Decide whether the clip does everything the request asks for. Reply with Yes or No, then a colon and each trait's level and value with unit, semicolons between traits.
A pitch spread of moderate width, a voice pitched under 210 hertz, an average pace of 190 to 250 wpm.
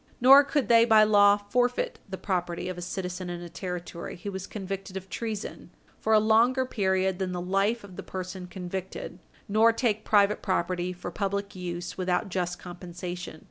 No: average, 3.0 semitones; high, 190 Hz; average, 180 wpm